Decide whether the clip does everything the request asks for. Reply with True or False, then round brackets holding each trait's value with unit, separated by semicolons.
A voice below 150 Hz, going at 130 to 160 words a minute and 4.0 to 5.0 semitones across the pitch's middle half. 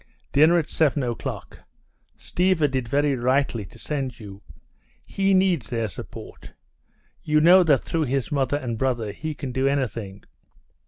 True (135 Hz; 150 wpm; 4.6 semitones)